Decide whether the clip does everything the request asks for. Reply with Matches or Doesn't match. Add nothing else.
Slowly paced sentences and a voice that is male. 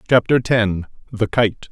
Matches